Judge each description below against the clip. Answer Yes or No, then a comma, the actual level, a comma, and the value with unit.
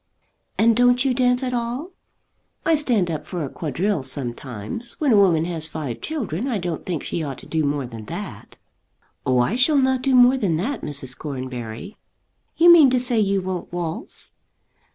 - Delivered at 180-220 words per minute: Yes, average, 185 wpm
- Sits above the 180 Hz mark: Yes, high, 190 Hz